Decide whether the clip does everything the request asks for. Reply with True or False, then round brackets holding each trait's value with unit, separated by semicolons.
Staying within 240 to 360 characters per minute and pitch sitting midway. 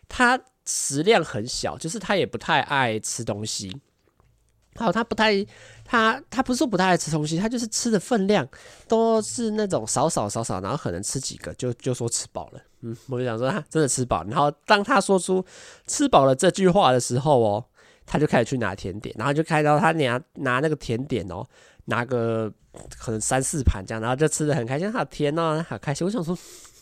True (295 characters per minute; 145 Hz)